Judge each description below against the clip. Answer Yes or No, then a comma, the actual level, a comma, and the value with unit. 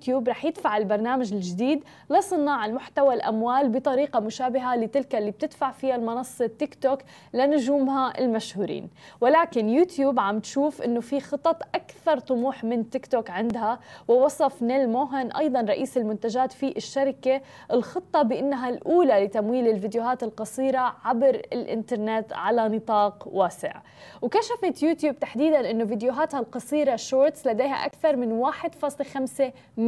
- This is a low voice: No, very high, 260 Hz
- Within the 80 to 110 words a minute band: No, average, 125 wpm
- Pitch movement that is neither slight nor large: Yes, average, 3.4 semitones